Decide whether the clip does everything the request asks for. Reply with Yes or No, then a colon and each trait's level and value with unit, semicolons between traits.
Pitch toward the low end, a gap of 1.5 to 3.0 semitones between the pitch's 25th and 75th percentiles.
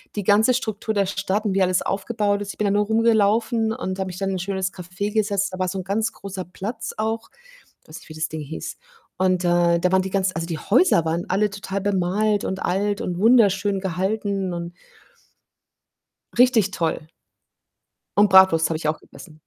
No: high, 195 Hz; narrow, 2.4 semitones